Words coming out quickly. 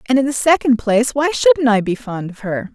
Yes: fast, 260 wpm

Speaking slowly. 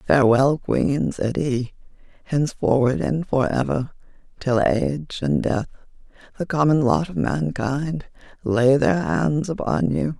Yes: slow, 130 wpm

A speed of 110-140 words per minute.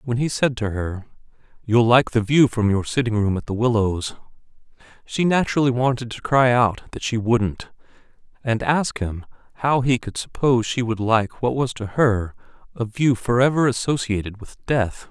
No: average, 185 wpm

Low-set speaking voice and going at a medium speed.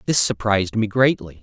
Yes: low, 110 Hz; average, 170 wpm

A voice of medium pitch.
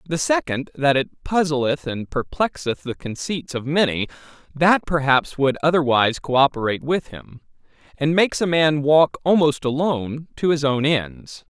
Yes: medium, 145 Hz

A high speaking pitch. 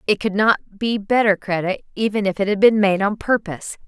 Yes: high, 205 Hz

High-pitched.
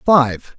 No: low, 135 Hz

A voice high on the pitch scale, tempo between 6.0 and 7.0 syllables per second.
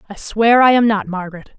Yes: high, 210 Hz; 6.1 syllables/s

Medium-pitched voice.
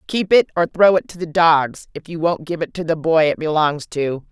Yes: medium, 165 Hz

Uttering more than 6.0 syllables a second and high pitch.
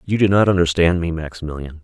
No: 6.4 syllables/s; very low, 85 Hz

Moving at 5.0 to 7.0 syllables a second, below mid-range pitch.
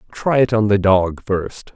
No: 4.0 syllables/s; low, 105 Hz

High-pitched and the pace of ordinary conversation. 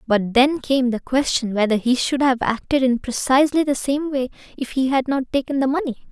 No: very high, 265 Hz; fast, 215 wpm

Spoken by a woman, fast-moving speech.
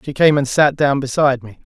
No: male; fast, 240 wpm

